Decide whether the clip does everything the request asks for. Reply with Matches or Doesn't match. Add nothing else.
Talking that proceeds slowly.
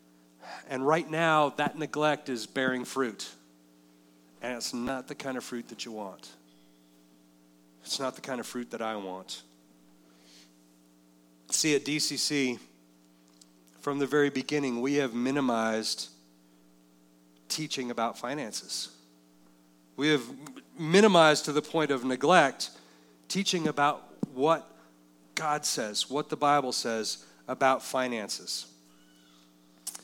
Matches